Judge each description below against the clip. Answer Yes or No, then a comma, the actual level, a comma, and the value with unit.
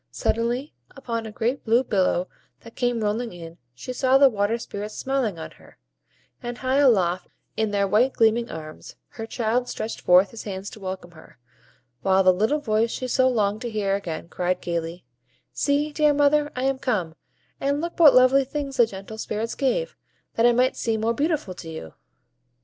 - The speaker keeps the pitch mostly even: No, average, 4.9 semitones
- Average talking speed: Yes, average, 185 wpm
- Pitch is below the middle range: No, high, 230 Hz